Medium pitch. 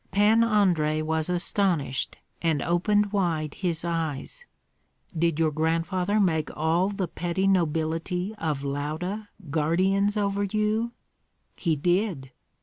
Yes: medium, 175 Hz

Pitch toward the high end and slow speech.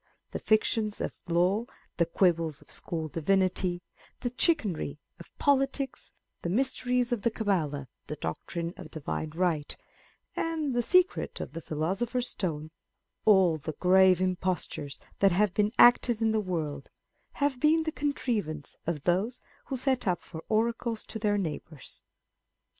No: high, 195 Hz; average, 150 wpm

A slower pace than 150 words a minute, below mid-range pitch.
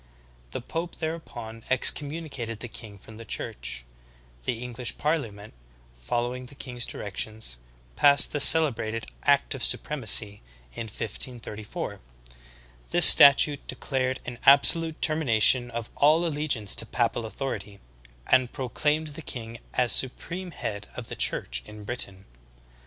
Yes: slow, 135 wpm; low, 125 Hz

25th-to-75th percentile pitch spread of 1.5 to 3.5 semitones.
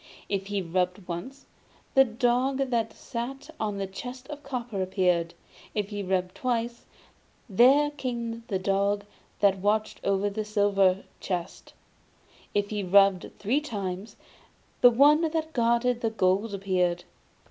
No: average, 4.2 semitones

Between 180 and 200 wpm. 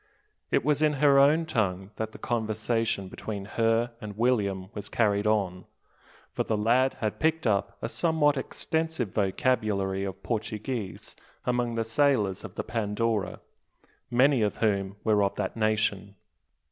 No: average, 145 wpm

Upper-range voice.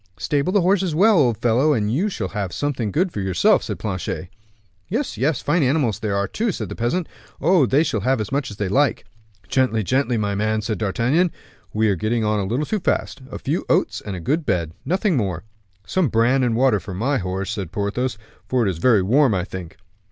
No: low, 115 Hz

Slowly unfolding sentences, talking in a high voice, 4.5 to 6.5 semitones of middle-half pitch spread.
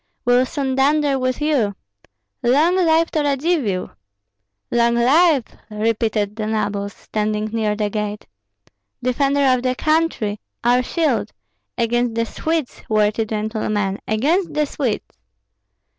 Yes: slow, 120 wpm; high, 240 Hz; average, 5.1 semitones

